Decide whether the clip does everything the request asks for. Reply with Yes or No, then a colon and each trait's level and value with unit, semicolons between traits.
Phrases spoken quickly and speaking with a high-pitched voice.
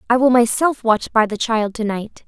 Yes: fast, 235 wpm; high, 230 Hz